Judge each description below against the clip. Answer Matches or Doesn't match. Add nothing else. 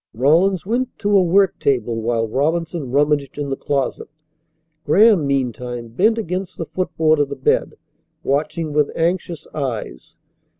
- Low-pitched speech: Doesn't match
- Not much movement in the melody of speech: Doesn't match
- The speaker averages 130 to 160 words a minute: Matches